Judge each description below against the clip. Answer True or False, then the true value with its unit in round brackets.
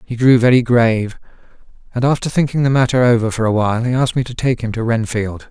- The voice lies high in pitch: False (120 Hz)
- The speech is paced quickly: True (220 wpm)